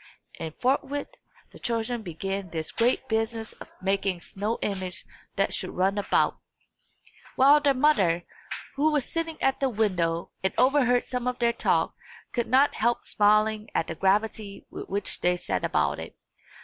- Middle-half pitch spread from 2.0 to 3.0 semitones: No, average, 4.7 semitones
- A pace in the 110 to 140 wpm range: No, average, 160 wpm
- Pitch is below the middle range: No, high, 220 Hz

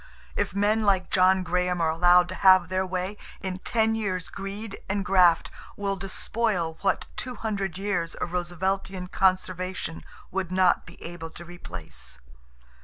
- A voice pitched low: No, medium, 185 Hz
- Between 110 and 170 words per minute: Yes, average, 150 wpm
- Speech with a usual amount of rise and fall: No, narrow, 1.9 semitones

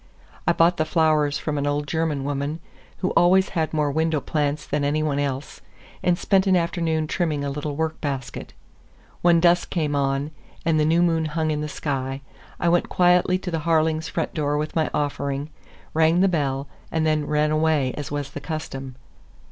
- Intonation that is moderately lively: No, narrow, 2.3 semitones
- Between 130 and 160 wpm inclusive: No, average, 190 wpm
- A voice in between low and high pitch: Yes, medium, 155 Hz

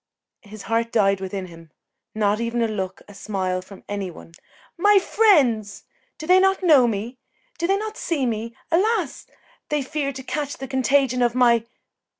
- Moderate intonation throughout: No, wide, 6.6 semitones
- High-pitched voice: Yes, high, 240 Hz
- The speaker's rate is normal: Yes, average, 170 wpm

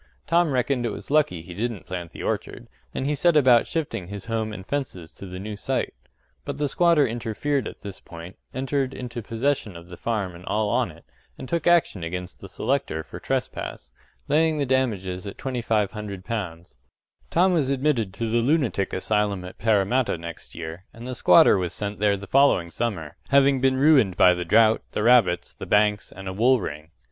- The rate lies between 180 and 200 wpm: Yes, average, 190 wpm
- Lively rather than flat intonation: Yes, wide, 6.2 semitones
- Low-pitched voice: Yes, low, 110 Hz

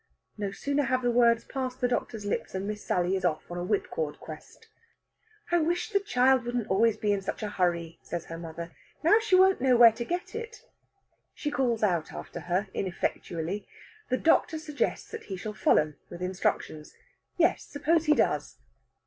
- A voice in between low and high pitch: No, high, 220 Hz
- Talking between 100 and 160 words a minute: No, average, 185 wpm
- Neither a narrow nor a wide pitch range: No, wide, 7.7 semitones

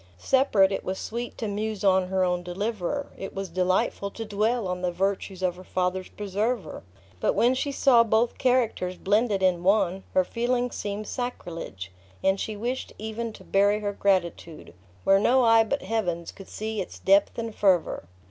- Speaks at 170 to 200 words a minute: Yes, average, 175 wpm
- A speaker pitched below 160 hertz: No, high, 200 Hz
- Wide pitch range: No, average, 3.5 semitones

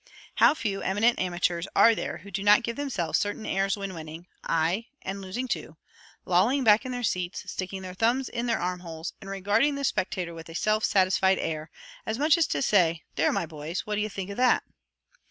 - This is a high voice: Yes, high, 195 Hz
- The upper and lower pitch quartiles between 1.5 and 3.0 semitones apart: No, average, 4.4 semitones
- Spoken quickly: Yes, fast, 210 wpm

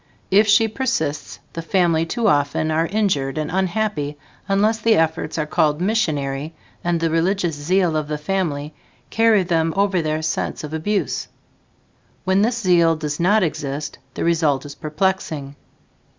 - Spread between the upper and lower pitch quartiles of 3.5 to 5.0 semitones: Yes, average, 4.4 semitones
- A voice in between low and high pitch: Yes, medium, 165 Hz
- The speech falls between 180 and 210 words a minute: No, average, 150 wpm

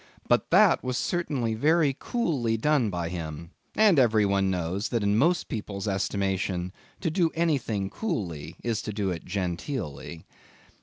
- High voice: No, low, 105 Hz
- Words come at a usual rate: Yes, average, 150 wpm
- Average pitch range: No, wide, 7.3 semitones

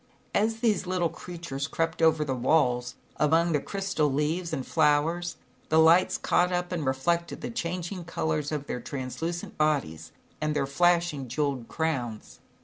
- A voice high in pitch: No, medium, 160 Hz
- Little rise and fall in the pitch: No, average, 3.8 semitones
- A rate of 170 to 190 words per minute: No, average, 150 wpm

